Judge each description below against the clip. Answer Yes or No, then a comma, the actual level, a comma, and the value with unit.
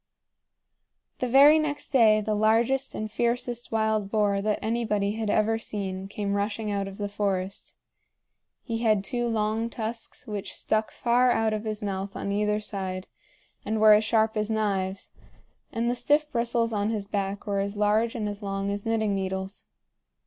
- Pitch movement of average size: No, narrow, 2.1 semitones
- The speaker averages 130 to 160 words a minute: No, average, 170 wpm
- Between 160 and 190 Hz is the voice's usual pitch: No, high, 215 Hz